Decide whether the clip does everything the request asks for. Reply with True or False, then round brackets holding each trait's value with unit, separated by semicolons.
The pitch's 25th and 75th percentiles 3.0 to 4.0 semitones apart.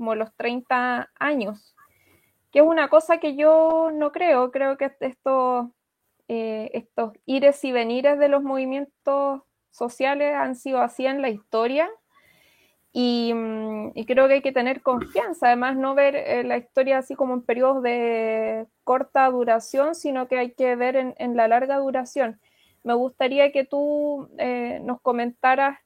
False (2.5 semitones)